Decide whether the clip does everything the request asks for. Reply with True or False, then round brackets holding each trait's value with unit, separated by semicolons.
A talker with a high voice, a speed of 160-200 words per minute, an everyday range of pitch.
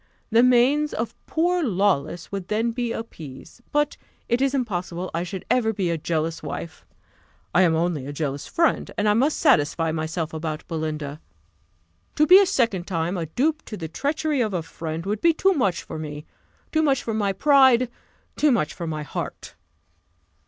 False (195 Hz; 180 wpm; 8.1 semitones)